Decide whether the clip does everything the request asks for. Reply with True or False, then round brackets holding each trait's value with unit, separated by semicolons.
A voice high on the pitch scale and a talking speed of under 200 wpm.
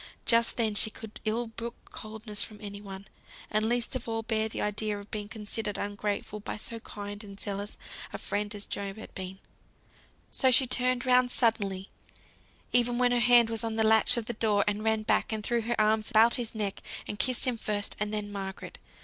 False (220 Hz; 205 wpm)